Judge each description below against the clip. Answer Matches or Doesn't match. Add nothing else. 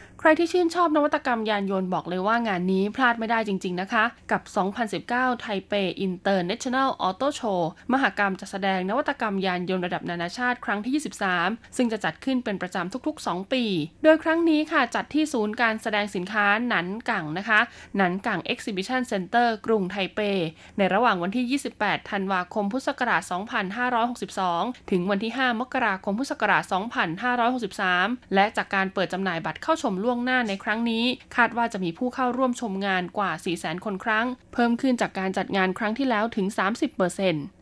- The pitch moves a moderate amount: Matches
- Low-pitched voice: Doesn't match